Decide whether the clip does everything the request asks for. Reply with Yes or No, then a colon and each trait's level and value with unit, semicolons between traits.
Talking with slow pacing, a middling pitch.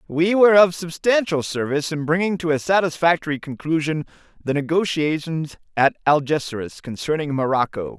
Yes: slow, 130 wpm; medium, 160 Hz